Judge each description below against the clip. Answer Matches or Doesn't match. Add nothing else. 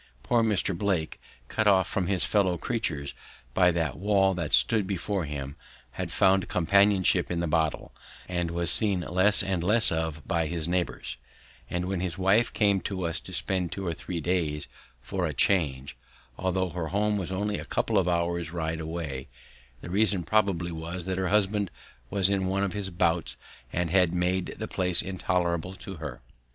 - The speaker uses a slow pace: Doesn't match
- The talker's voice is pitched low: Matches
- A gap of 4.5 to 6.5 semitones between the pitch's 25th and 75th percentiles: Doesn't match